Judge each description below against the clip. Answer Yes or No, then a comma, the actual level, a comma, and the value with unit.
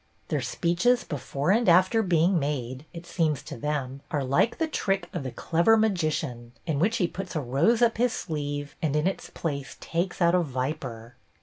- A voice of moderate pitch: Yes, medium, 160 Hz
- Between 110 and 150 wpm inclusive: No, average, 190 wpm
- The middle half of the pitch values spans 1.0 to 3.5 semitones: No, average, 5.1 semitones